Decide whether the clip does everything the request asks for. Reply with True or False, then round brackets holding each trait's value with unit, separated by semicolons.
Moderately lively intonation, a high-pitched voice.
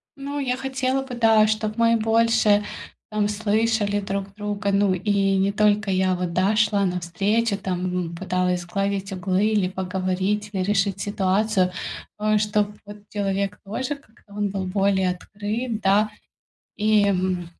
False (2.1 semitones; 205 Hz)